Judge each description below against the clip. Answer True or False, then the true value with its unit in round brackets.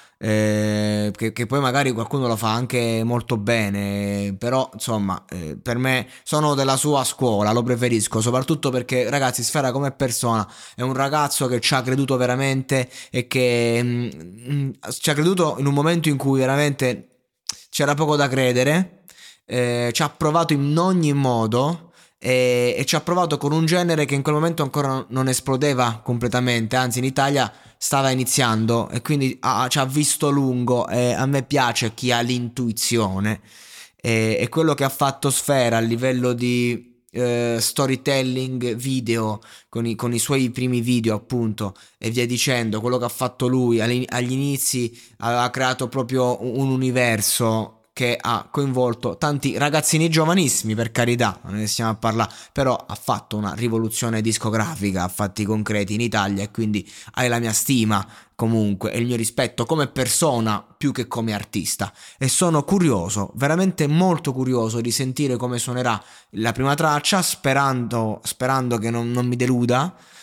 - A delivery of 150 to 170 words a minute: True (160 wpm)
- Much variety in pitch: False (3.1 semitones)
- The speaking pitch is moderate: False (125 Hz)